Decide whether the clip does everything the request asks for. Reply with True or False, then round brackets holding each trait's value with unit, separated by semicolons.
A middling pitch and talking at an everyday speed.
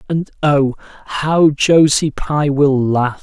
False (145 Hz; 130 wpm)